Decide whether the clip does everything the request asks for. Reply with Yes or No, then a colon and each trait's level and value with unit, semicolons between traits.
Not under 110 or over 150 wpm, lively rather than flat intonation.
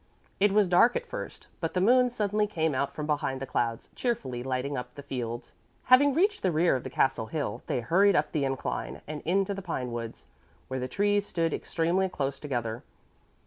No: average, 195 wpm; wide, 7.4 semitones